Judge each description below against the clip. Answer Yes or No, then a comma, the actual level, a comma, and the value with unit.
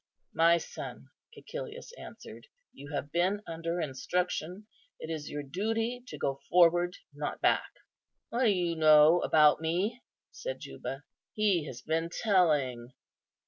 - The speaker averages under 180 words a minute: Yes, slow, 135 wpm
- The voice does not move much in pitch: No, average, 5.0 semitones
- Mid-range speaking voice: Yes, medium, 170 Hz